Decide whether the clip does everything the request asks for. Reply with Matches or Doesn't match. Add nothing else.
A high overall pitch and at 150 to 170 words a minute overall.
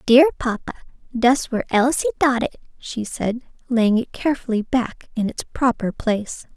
Matches